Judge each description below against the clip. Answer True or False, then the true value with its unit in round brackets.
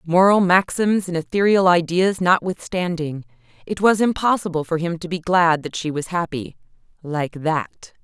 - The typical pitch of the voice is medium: True (175 Hz)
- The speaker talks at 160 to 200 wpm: False (140 wpm)